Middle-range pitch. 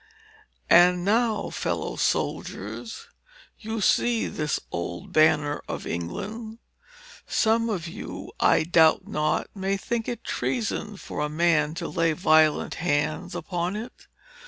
Yes: medium, 175 Hz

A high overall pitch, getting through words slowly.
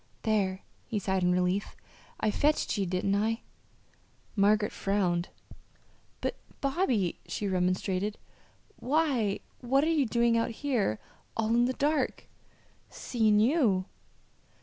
Yes: high, 215 Hz; slow, 120 wpm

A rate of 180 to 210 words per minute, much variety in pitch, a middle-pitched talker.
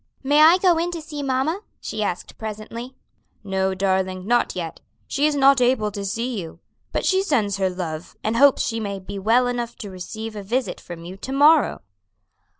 No: average, 195 wpm; wide, 6.0 semitones; high, 225 Hz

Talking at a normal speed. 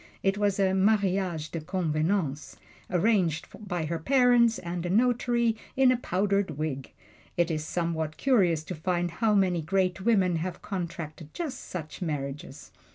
Yes: average, 150 wpm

